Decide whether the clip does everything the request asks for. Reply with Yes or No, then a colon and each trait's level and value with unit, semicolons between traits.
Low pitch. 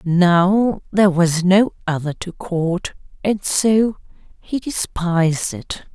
No: medium, 185 Hz